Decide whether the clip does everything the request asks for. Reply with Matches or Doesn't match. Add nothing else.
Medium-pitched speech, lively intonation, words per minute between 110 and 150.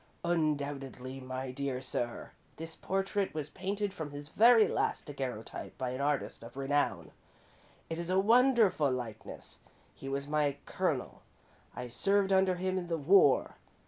Matches